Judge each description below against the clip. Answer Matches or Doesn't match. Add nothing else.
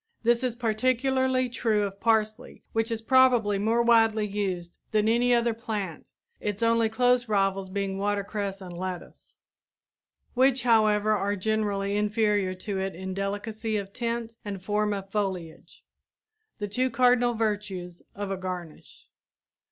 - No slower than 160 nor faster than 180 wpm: Doesn't match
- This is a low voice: Doesn't match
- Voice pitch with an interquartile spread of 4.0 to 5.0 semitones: Doesn't match